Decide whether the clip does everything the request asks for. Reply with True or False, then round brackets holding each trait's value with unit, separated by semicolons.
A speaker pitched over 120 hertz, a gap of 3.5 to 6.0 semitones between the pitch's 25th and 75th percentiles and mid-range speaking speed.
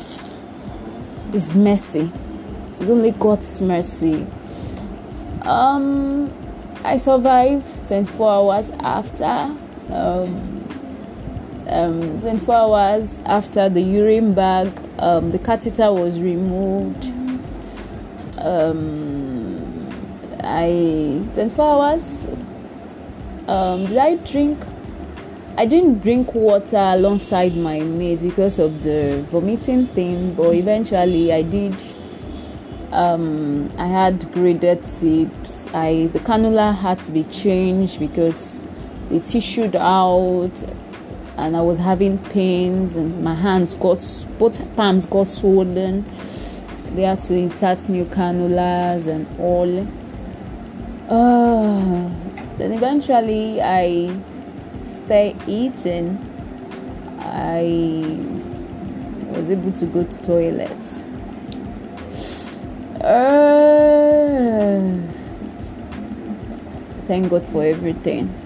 False (185 Hz; 4.1 semitones; 95 wpm)